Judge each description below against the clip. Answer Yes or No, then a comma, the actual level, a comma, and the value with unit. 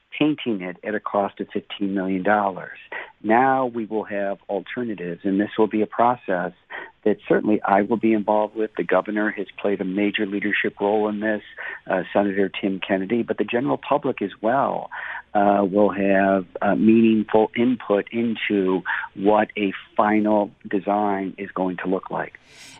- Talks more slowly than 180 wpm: Yes, average, 165 wpm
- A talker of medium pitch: No, low, 105 Hz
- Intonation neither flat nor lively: No, narrow, 1.7 semitones